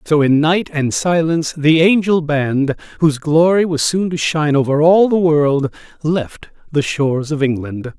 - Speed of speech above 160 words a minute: Yes, average, 175 wpm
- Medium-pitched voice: Yes, medium, 155 Hz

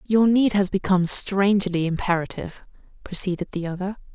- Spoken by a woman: Yes, female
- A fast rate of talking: No, slow, 130 wpm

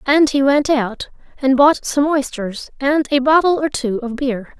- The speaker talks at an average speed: Yes, average, 195 wpm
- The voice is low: No, very high, 270 Hz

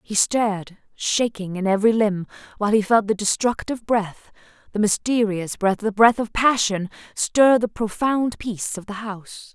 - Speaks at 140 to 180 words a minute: Yes, average, 165 wpm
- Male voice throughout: No, female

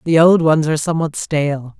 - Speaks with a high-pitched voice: No, medium, 155 Hz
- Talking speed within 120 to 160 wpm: No, average, 200 wpm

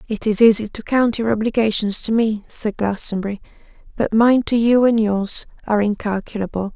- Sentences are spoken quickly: No, average, 170 wpm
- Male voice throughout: No, female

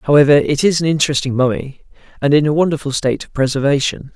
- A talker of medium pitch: Yes, medium, 145 Hz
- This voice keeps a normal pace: Yes, average, 190 wpm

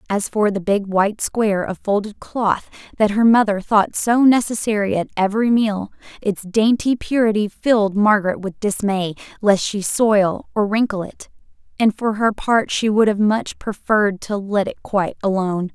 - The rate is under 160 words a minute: No, average, 170 wpm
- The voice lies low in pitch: No, high, 210 Hz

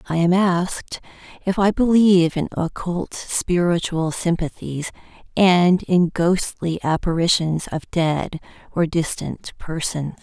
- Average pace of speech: No, slow, 110 wpm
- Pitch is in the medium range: Yes, medium, 175 Hz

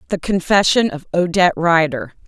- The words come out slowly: Yes, slow, 130 wpm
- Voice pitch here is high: No, medium, 170 Hz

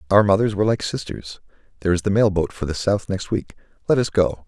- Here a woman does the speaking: No, male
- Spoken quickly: Yes, fast, 230 wpm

